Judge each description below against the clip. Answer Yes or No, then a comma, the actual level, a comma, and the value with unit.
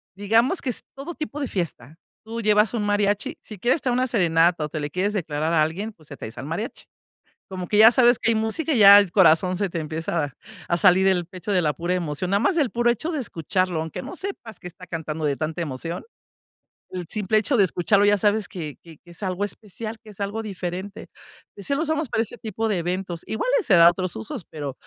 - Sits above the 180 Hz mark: Yes, high, 190 Hz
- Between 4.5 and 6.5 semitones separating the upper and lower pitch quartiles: Yes, average, 4.8 semitones